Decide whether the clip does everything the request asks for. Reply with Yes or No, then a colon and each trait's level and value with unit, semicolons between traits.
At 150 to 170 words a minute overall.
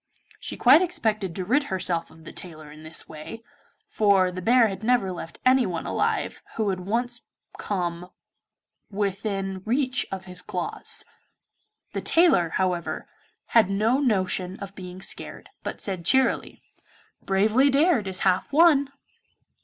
No: average, 140 wpm